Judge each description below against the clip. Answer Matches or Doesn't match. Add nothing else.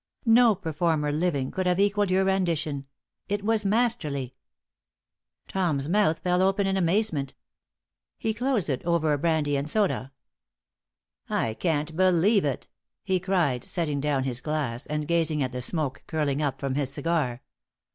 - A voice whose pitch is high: Doesn't match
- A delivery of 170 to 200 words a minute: Doesn't match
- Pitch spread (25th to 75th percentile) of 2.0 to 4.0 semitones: Doesn't match